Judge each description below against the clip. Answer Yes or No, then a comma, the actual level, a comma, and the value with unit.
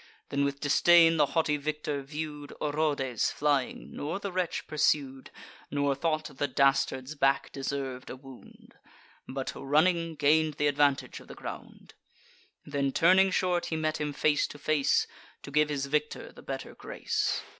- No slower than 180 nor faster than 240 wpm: No, average, 155 wpm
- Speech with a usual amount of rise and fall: No, narrow, 2.1 semitones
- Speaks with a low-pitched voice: No, medium, 145 Hz